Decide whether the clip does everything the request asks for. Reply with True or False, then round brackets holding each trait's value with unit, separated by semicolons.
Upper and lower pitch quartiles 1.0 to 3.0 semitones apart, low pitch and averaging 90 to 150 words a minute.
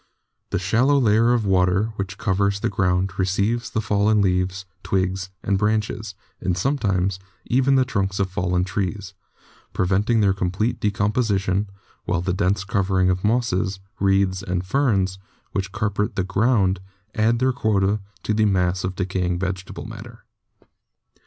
True (2.5 semitones; 100 Hz; 145 wpm)